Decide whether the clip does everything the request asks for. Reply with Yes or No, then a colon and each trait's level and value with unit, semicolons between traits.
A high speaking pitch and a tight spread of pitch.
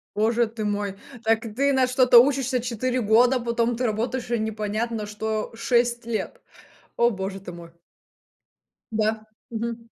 Yes: high, 230 Hz; narrow, 2.1 semitones